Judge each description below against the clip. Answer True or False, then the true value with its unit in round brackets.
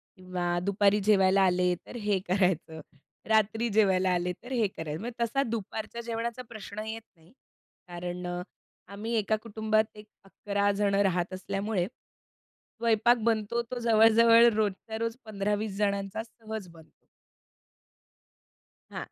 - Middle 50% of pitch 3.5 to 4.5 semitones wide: False (3.1 semitones)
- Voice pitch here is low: False (210 Hz)